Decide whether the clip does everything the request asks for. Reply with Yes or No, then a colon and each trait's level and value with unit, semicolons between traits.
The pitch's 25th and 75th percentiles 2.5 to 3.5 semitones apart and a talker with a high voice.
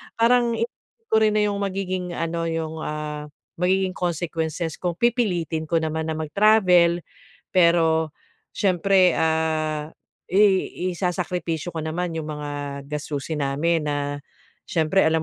No: average, 2.9 semitones; medium, 170 Hz